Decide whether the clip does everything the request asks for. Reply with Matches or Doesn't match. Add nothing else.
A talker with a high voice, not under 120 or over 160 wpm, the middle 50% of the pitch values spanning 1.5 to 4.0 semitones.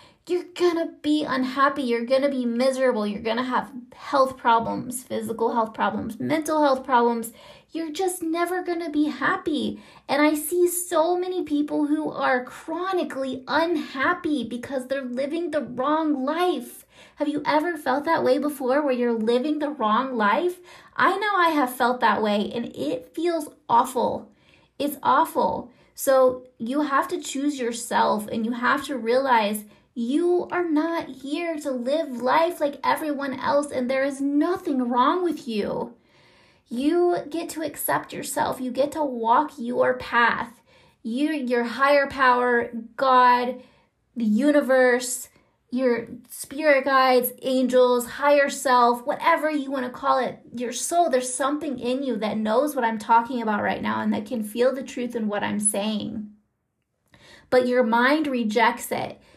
Matches